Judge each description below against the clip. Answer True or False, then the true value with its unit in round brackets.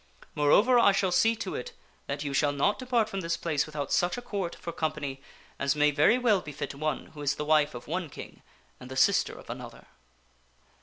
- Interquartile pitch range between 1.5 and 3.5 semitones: False (5.6 semitones)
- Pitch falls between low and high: True (155 Hz)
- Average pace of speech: False (210 wpm)